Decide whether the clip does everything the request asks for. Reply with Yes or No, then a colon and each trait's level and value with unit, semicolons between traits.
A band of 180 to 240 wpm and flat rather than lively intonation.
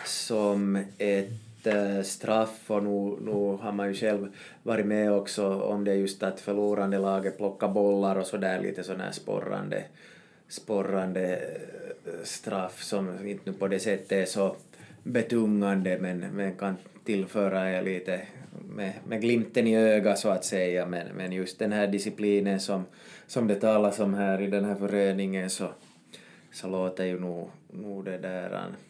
No: average, 165 wpm; narrow, 1.4 semitones